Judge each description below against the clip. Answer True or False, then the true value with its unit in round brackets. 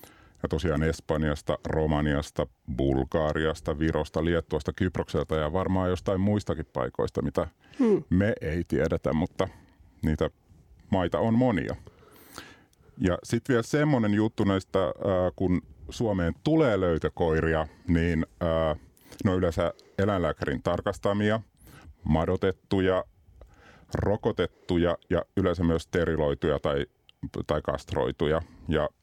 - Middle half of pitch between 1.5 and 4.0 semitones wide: True (3.4 semitones)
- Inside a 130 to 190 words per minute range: False (95 wpm)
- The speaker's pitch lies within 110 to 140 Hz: False (85 Hz)